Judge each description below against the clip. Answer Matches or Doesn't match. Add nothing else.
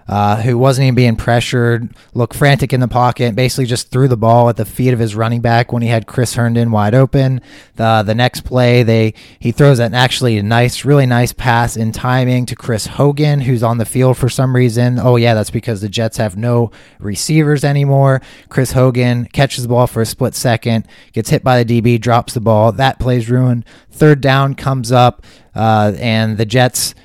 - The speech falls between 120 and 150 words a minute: Doesn't match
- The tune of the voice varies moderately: Doesn't match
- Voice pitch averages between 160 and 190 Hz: Doesn't match